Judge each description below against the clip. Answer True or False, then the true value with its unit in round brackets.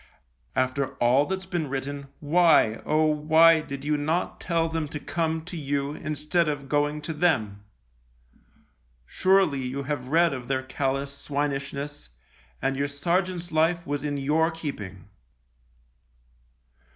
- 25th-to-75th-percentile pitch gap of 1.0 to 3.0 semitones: True (2.7 semitones)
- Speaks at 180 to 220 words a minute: False (135 wpm)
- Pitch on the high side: False (145 Hz)